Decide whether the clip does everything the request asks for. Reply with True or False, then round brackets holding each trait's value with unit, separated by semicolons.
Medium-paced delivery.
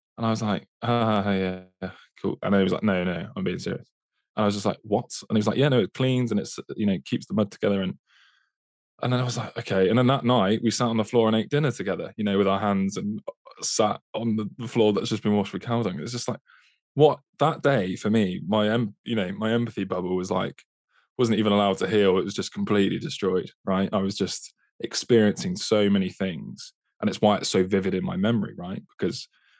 False (245 wpm)